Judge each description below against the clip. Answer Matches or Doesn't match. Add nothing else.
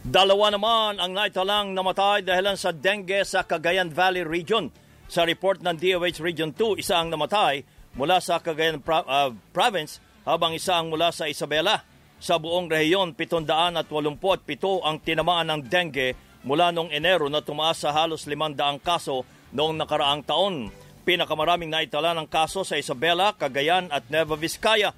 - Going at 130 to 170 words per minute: Matches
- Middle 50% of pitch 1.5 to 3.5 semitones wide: Matches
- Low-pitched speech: Doesn't match